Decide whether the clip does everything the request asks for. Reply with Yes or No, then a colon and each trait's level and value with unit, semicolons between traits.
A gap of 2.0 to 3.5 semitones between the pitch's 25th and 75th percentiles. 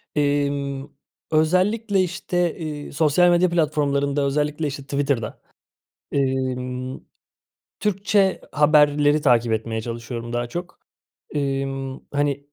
Yes: average, 2.8 semitones